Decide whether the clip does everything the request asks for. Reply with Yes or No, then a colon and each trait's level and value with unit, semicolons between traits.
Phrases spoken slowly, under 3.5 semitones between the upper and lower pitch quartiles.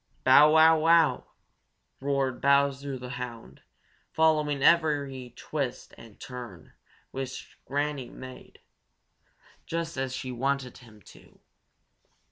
Yes: slow, 105 wpm; average, 2.9 semitones